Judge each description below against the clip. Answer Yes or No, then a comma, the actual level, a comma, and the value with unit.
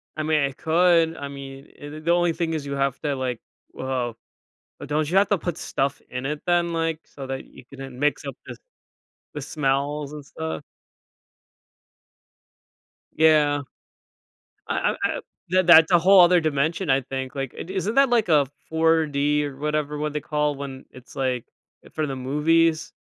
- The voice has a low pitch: No, medium, 150 Hz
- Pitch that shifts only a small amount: No, average, 3.0 semitones